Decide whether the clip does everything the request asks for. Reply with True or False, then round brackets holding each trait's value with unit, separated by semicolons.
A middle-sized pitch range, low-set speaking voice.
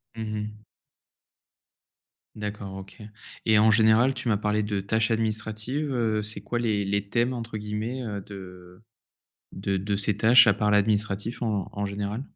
False (1.7 semitones; 105 Hz)